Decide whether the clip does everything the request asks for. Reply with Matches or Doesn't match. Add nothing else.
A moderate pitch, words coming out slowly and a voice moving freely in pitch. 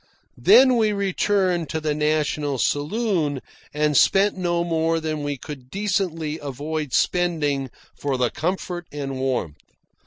Doesn't match